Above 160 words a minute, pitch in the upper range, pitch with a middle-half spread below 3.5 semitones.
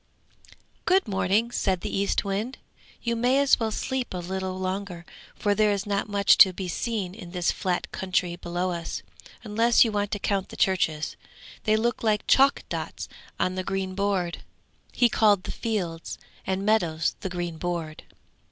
Yes: average, 170 wpm; high, 195 Hz; average, 3.1 semitones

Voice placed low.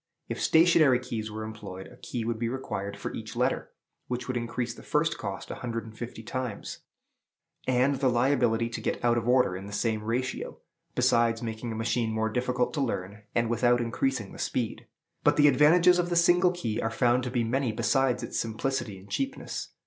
Yes: low, 120 Hz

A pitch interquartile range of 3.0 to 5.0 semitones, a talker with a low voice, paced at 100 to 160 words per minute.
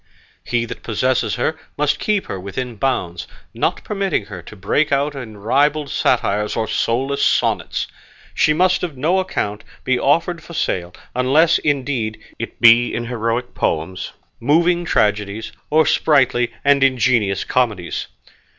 No: wide, 5.5 semitones; low, 125 Hz; average, 140 wpm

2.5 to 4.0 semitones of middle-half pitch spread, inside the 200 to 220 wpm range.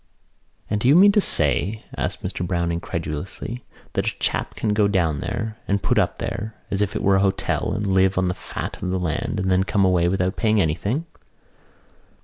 Yes: average, 3.0 semitones; fast, 205 wpm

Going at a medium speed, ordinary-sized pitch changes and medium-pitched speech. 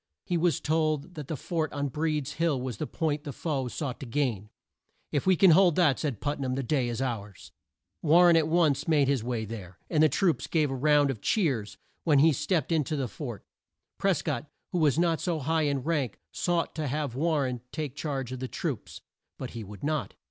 No: fast, 220 wpm; average, 3.8 semitones; medium, 145 Hz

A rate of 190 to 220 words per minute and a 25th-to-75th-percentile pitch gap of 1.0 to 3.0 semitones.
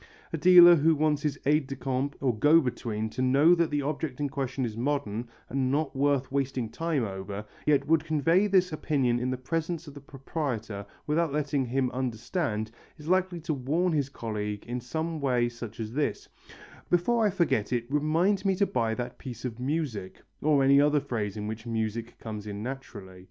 No: average, 195 wpm; average, 4.8 semitones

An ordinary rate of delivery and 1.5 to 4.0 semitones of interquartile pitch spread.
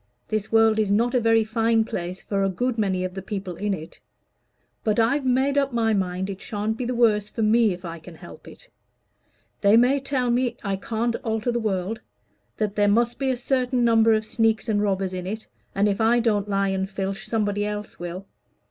No: fast, 215 wpm; average, 3.2 semitones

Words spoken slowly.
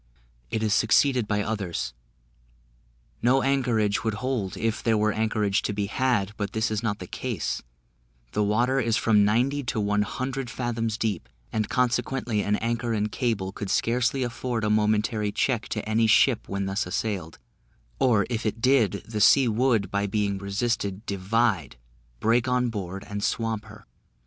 No: average, 165 wpm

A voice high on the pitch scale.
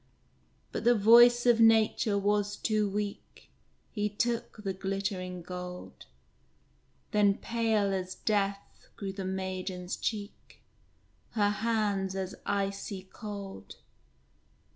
Yes: high, 200 Hz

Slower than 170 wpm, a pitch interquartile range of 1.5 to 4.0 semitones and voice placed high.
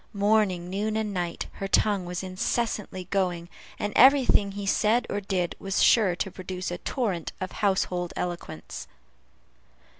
Yes: average, 150 wpm; average, 2.7 semitones; high, 195 Hz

